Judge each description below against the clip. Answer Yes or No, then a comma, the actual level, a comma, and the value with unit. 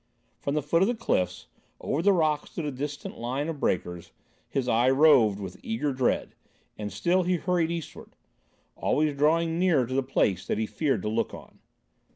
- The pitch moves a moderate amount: No, wide, 6.1 semitones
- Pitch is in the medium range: Yes, medium, 145 Hz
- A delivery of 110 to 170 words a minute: No, average, 190 wpm